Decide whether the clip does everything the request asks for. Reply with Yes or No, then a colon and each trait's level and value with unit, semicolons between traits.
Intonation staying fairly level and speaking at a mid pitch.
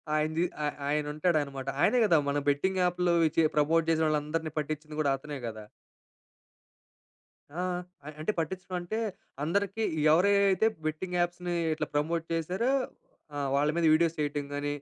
No: average, 3.1 semitones; medium, 160 Hz